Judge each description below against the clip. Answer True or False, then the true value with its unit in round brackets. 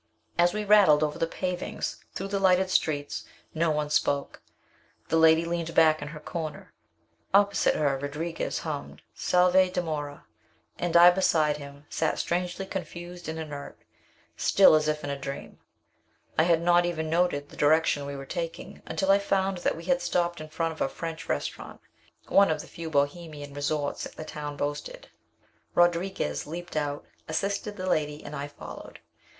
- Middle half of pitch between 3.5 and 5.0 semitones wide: False (3.0 semitones)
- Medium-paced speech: True (165 wpm)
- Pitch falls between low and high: True (160 Hz)